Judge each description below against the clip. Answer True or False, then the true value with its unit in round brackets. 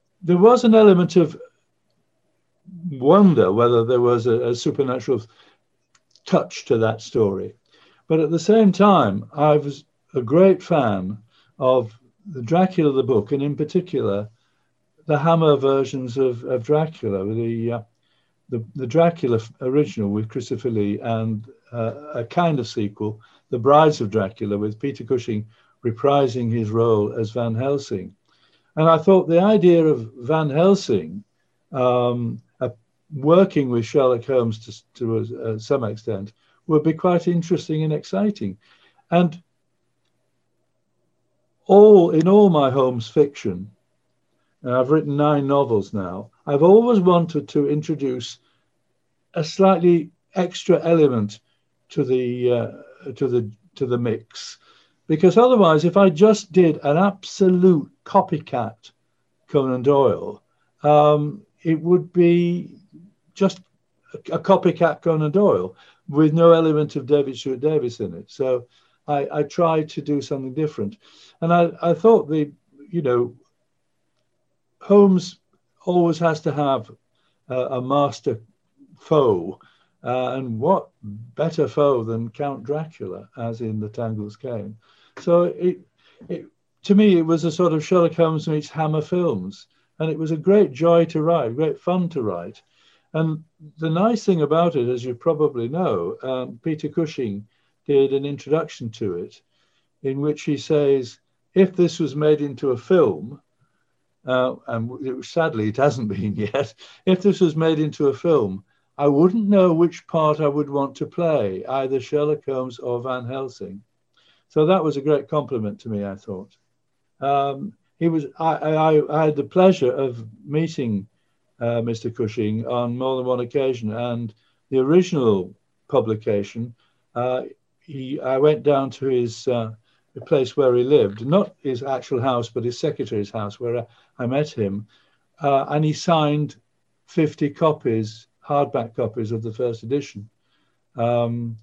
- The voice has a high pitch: False (145 Hz)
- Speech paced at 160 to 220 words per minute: False (145 wpm)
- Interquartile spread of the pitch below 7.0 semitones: True (5.3 semitones)